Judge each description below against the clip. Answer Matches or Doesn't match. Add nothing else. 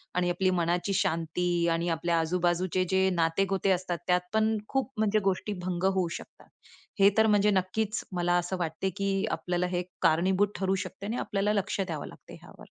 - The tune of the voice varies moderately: Doesn't match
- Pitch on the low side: Doesn't match